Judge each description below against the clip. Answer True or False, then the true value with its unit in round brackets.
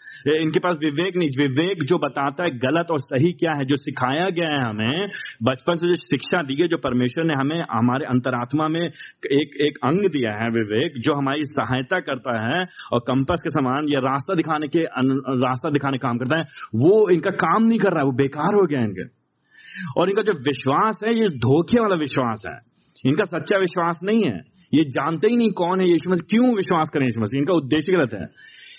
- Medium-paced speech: False (210 wpm)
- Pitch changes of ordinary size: True (4.9 semitones)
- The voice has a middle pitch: True (155 Hz)